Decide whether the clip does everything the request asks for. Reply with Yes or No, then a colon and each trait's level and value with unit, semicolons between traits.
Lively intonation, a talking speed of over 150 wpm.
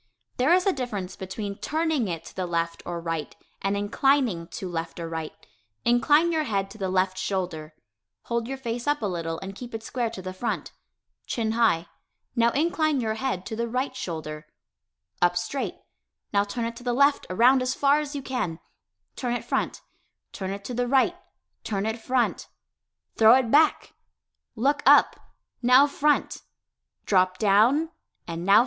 Yes: wide, 6.0 semitones; average, 180 wpm